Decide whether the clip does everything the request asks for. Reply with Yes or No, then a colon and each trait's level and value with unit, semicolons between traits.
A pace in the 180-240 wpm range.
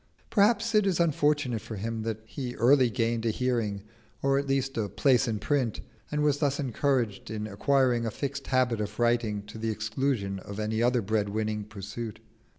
Yes: average, 185 wpm